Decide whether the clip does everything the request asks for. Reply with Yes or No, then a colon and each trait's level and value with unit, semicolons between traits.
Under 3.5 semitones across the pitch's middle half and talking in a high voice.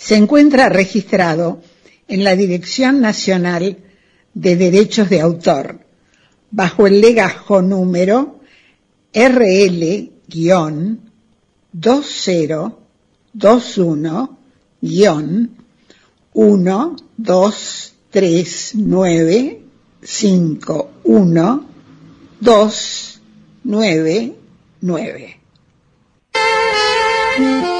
No: average, 4.3 semitones; high, 205 Hz